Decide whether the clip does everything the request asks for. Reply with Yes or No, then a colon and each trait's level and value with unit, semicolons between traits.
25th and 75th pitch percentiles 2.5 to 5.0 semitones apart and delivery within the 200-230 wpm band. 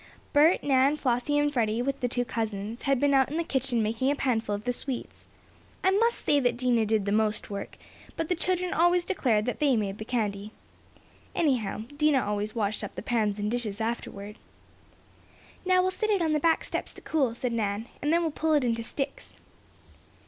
No: wide, 5.4 semitones; fast, 205 wpm